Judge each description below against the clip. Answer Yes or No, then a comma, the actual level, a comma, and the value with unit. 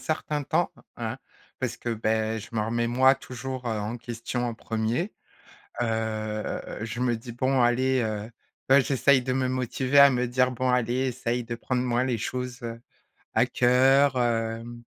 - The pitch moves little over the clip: Yes, narrow, 2.1 semitones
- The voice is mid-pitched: No, low, 120 Hz